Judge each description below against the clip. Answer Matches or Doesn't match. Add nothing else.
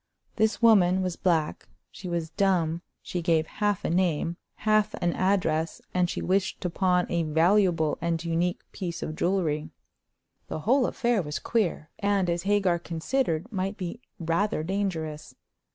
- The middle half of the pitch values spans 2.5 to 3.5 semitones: Matches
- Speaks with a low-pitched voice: Doesn't match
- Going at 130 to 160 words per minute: Matches